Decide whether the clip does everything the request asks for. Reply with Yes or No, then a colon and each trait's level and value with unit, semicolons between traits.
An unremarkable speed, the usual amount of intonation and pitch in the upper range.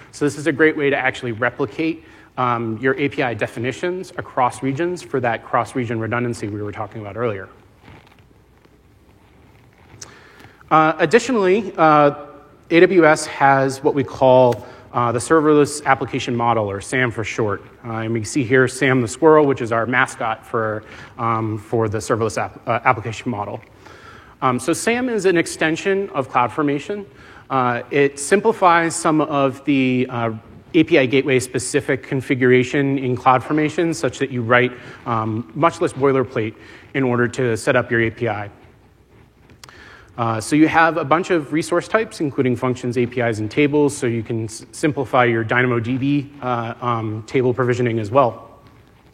No: average, 155 wpm; average, 4.2 semitones; low, 130 Hz